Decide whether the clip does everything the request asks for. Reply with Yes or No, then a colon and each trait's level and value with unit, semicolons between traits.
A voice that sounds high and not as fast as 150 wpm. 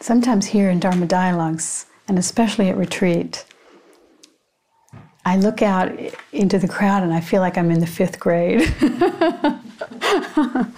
Yes: high, 195 Hz; slow, 135 wpm